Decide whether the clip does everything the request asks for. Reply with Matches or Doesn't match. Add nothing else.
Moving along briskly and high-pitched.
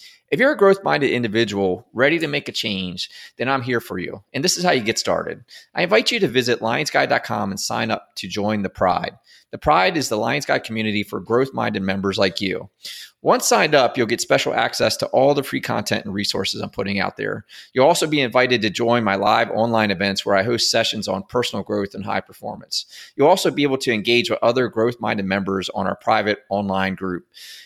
Doesn't match